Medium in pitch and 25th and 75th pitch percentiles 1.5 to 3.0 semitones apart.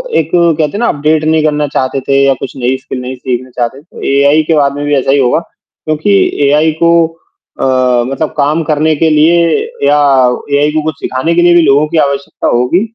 Yes: medium, 150 Hz; narrow, 2.5 semitones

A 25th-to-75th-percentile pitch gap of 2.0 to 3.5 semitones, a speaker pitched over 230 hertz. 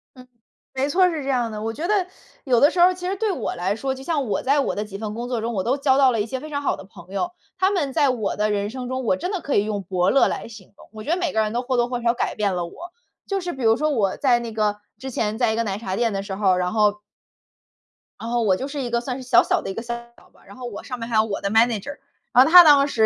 No: average, 4.6 semitones; high, 240 Hz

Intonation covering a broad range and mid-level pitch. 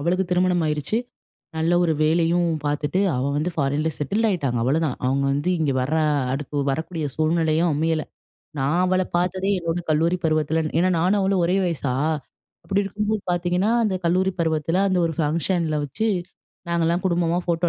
No: average, 3.0 semitones; medium, 165 Hz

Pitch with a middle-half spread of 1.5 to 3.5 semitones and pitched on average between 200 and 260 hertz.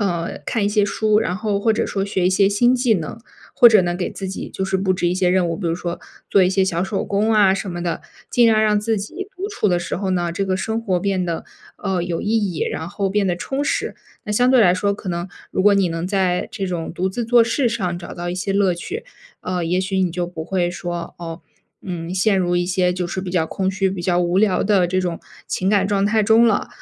No: average, 2.8 semitones; high, 190 Hz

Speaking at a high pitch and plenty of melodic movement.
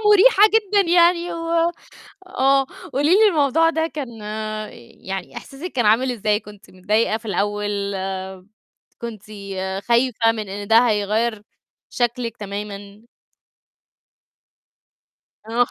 Yes: high, 235 Hz; wide, 6.2 semitones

